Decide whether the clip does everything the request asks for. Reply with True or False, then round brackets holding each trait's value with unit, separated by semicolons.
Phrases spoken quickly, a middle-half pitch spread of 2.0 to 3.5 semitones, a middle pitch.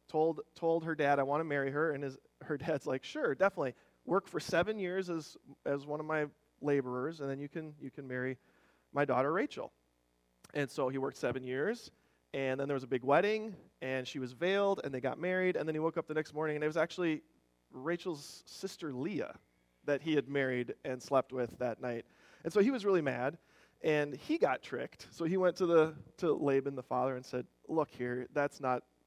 False (220 wpm; 4.0 semitones; 145 Hz)